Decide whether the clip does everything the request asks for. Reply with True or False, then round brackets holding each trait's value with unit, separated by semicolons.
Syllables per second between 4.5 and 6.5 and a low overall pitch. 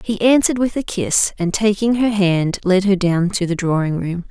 False (4.9 syllables/s; 195 Hz)